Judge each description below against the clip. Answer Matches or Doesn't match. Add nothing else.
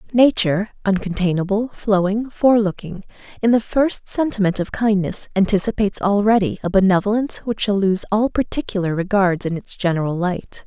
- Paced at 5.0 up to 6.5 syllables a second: Matches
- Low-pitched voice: Doesn't match